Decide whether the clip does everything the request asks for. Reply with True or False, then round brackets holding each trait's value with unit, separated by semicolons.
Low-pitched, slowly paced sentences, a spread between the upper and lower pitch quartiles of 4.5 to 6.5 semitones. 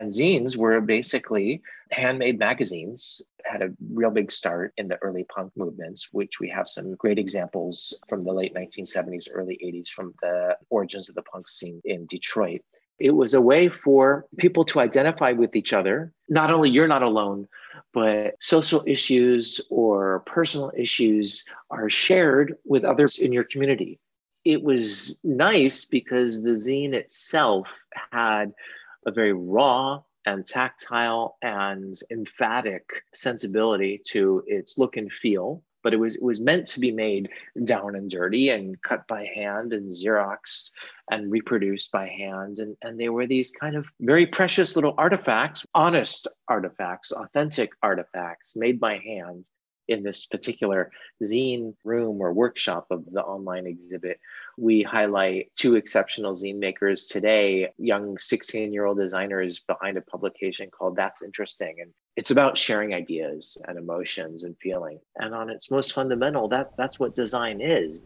False (110 Hz; 155 wpm; 5.3 semitones)